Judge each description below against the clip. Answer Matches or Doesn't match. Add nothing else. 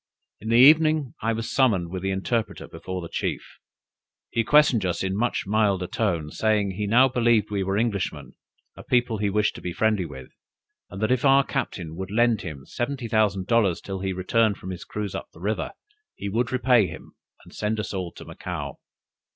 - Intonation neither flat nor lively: Matches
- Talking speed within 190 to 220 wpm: Matches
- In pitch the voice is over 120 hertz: Doesn't match